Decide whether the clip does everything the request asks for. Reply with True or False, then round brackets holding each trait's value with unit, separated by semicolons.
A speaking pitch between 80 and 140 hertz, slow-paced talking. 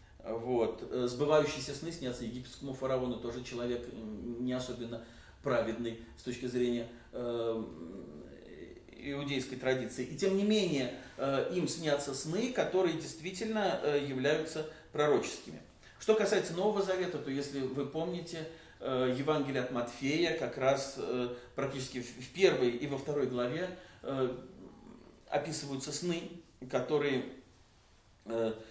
False (135 Hz; 120 wpm)